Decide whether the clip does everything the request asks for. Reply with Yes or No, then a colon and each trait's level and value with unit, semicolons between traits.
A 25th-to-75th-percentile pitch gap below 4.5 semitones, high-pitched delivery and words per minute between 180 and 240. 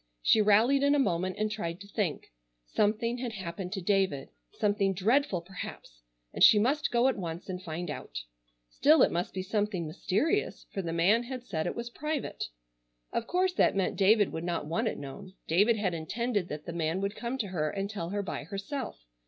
No: average, 5.2 semitones; high, 200 Hz; average, 200 wpm